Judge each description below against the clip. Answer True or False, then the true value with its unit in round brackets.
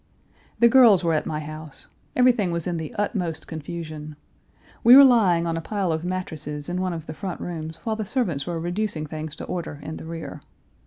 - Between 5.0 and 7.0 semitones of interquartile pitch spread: False (3.9 semitones)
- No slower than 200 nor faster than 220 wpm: True (205 wpm)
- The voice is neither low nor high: True (170 Hz)